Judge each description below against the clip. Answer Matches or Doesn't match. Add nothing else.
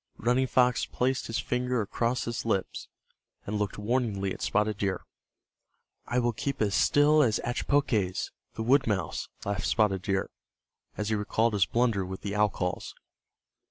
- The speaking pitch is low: Matches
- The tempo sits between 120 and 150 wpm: Doesn't match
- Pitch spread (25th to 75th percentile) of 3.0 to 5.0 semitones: Matches